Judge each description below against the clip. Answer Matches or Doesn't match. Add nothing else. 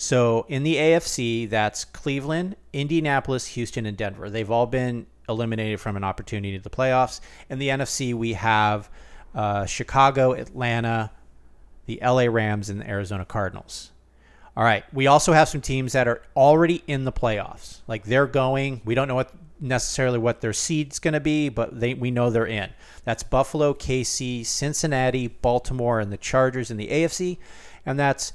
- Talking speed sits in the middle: Matches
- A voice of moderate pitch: Doesn't match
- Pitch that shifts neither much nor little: Matches